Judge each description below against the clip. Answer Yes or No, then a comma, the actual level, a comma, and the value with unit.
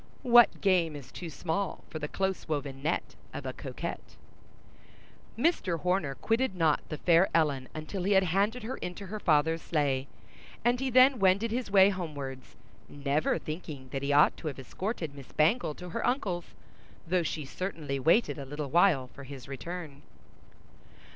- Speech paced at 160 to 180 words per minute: Yes, average, 165 wpm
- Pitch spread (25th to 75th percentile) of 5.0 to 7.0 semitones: Yes, average, 5.3 semitones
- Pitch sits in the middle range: Yes, medium, 165 Hz